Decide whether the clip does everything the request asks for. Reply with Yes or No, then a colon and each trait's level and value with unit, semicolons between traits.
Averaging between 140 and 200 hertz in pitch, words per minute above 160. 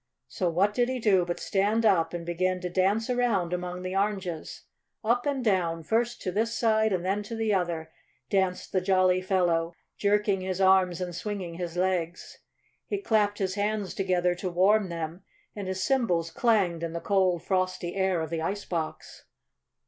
Yes: medium, 185 Hz; average, 180 wpm